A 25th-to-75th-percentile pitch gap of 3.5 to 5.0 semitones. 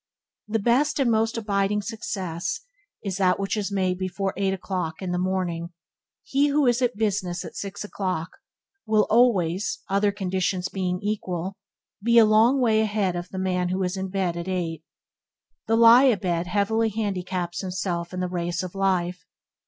No: average, 3.0 semitones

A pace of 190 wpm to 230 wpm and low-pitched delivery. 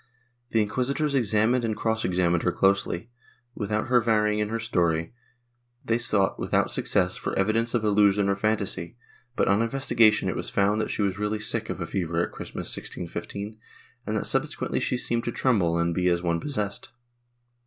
No: average, 180 wpm; low, 105 Hz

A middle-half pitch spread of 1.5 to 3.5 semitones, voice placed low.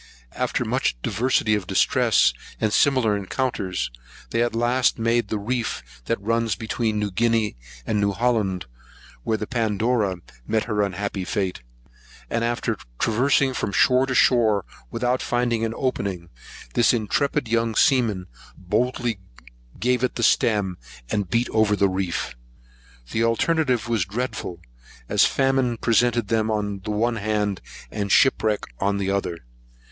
Yes: average, 2.9 semitones; low, 110 Hz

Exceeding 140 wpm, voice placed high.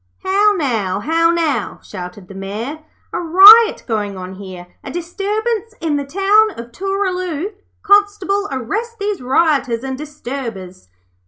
No: slow, 135 wpm; very high, 315 Hz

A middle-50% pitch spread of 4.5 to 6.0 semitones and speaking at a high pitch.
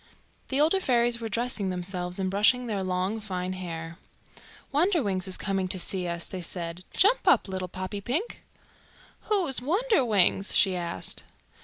Yes: average, 5.3 semitones; high, 195 Hz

